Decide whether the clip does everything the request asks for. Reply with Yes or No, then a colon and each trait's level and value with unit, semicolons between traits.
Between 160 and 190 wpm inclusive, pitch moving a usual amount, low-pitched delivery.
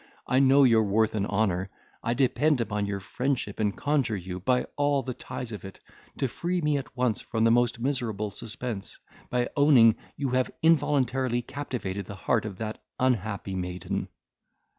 Yes: average, 170 wpm; average, 4.4 semitones; low, 120 Hz